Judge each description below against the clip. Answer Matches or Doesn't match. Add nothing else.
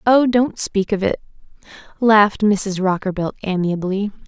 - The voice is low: Doesn't match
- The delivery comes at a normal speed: Doesn't match